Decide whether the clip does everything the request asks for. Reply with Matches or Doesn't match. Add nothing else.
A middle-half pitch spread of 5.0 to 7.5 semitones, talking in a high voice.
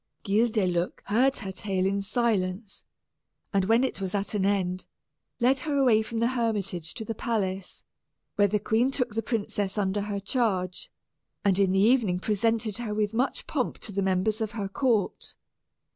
Doesn't match